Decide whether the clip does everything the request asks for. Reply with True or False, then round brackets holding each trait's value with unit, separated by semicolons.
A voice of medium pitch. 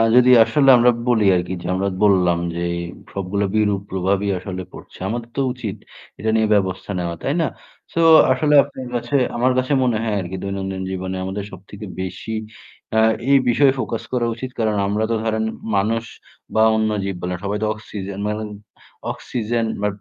False (105 Hz)